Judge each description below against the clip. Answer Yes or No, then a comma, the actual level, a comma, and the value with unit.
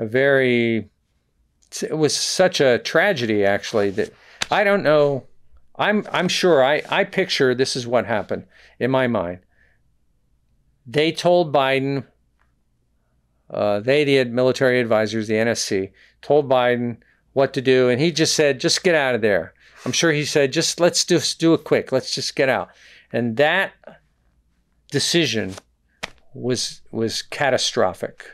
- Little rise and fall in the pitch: No, wide, 5.9 semitones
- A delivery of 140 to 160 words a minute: Yes, average, 150 wpm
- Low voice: Yes, low, 130 Hz